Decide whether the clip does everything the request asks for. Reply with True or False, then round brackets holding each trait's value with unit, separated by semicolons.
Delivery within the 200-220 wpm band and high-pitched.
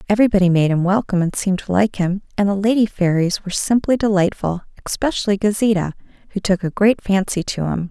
False (190 wpm; 195 Hz)